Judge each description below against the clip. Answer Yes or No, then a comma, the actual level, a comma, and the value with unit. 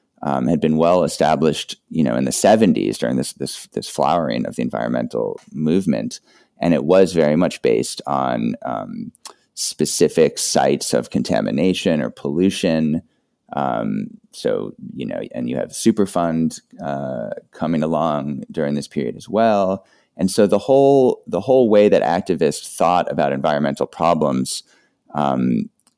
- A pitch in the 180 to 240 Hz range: No, low, 100 Hz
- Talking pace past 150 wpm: No, average, 145 wpm